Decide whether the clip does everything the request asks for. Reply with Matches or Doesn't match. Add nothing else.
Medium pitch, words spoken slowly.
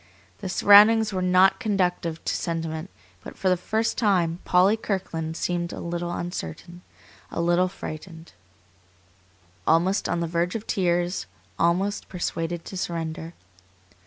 Matches